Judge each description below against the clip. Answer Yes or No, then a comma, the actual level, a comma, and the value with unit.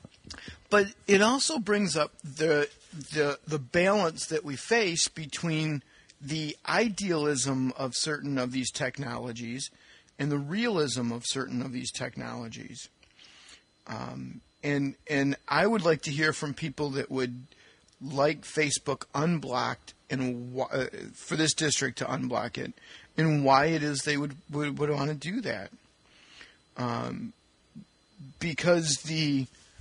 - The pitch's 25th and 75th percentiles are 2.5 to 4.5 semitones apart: Yes, average, 3.4 semitones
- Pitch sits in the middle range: Yes, medium, 145 Hz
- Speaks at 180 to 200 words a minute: No, slow, 135 wpm